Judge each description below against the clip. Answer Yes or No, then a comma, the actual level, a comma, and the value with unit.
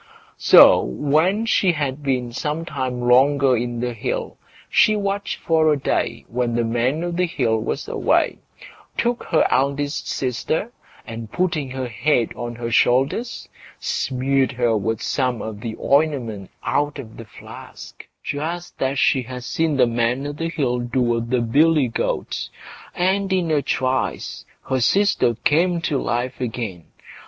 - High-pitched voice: No, low, 130 Hz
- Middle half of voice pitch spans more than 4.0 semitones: Yes, average, 4.6 semitones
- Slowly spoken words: No, average, 155 wpm